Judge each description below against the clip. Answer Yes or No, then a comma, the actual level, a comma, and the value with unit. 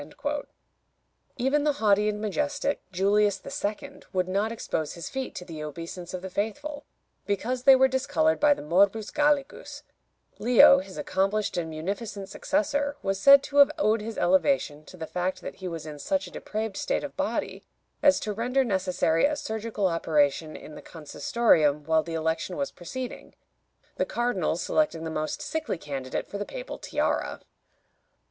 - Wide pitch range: Yes, wide, 7.8 semitones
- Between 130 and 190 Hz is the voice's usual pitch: No, high, 205 Hz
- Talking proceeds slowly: No, average, 165 wpm